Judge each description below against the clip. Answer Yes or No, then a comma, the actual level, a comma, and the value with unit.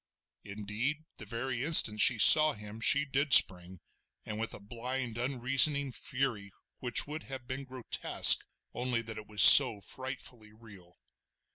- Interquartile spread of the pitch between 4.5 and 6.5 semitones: No, average, 3.9 semitones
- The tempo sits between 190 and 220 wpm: No, average, 145 wpm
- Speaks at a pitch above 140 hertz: No, low, 120 Hz